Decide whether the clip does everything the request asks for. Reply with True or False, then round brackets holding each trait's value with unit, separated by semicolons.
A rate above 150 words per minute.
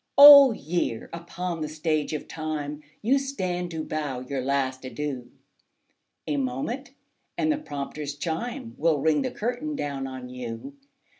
False (145 wpm)